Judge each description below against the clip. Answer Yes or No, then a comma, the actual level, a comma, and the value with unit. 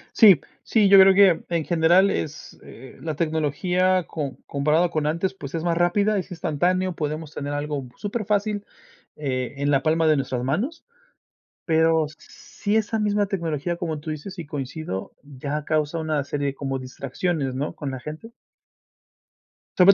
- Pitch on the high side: No, medium, 160 Hz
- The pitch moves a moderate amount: Yes, average, 4.3 semitones